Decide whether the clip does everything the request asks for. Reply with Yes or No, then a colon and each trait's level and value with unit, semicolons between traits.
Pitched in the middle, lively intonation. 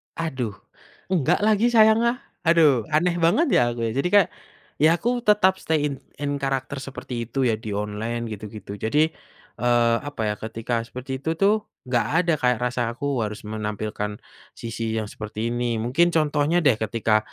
No: low, 130 Hz; wide, 6.5 semitones